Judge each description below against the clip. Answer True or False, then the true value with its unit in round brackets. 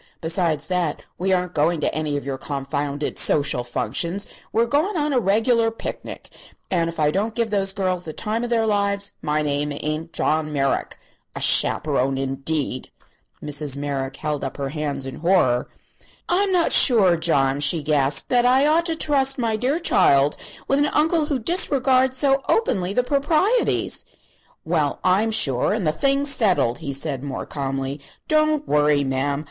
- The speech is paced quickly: False (170 wpm)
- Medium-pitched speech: True (170 Hz)